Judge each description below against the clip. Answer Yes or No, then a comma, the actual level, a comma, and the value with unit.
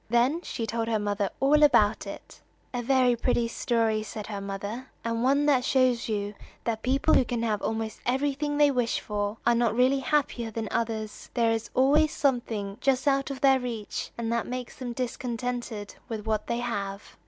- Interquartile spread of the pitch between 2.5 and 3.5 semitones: Yes, average, 2.9 semitones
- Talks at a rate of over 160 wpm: Yes, average, 190 wpm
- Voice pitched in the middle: No, high, 235 Hz